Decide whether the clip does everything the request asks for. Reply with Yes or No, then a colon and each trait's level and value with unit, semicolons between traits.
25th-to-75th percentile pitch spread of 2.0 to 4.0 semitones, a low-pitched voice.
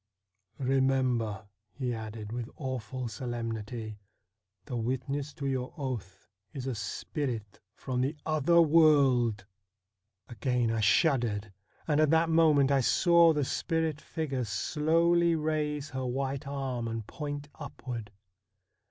No: average, 4.7 semitones; low, 130 Hz